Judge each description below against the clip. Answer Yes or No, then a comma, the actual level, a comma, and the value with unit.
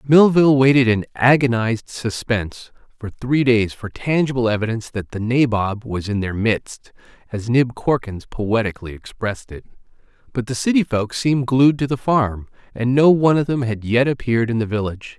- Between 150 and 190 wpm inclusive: Yes, average, 175 wpm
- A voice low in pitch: Yes, low, 120 Hz